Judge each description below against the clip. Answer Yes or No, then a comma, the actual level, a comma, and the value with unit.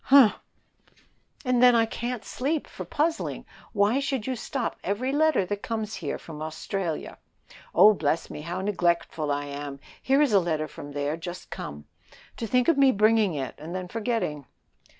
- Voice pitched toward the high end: Yes, high, 205 Hz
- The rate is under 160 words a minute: No, average, 170 wpm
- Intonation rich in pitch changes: Yes, wide, 7.8 semitones